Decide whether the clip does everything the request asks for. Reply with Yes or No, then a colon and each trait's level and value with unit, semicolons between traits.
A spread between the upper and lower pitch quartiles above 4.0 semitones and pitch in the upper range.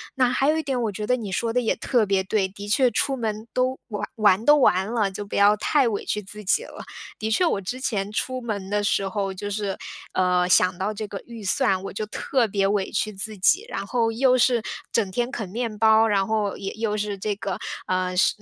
No: average, 3.2 semitones; high, 210 Hz